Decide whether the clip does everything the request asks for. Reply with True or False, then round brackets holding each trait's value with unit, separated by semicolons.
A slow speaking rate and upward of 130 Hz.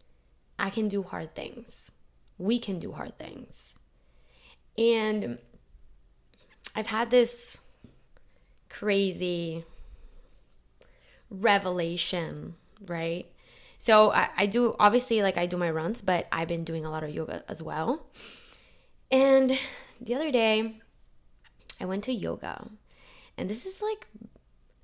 True (120 wpm; 190 Hz)